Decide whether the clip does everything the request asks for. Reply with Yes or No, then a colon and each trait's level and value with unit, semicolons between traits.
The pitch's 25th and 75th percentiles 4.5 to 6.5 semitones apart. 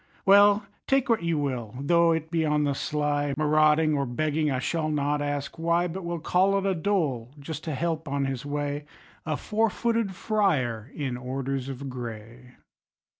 No: average, 3.7 semitones